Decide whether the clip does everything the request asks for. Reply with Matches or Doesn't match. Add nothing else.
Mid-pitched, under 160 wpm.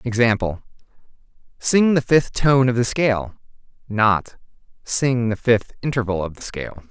Doesn't match